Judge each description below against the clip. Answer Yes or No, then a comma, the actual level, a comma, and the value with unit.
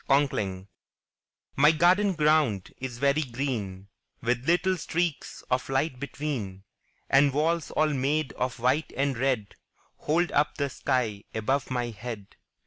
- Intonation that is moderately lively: Yes, average, 4.2 semitones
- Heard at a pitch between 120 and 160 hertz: Yes, low, 135 Hz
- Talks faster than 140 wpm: No, slow, 135 wpm